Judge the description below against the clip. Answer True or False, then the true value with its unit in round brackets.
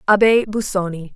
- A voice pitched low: False (195 Hz)